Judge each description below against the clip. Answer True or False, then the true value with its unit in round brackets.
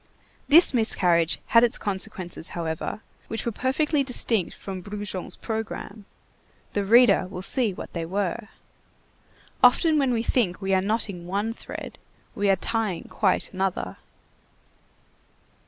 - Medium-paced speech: False (130 wpm)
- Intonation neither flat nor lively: True (3.9 semitones)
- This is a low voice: False (205 Hz)